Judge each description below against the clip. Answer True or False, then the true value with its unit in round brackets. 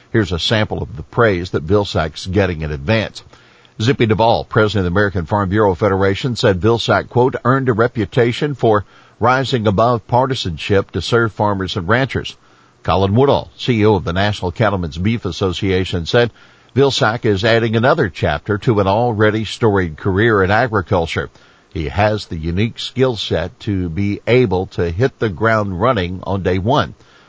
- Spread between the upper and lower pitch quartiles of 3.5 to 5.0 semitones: True (4.0 semitones)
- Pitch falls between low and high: False (105 Hz)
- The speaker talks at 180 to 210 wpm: False (165 wpm)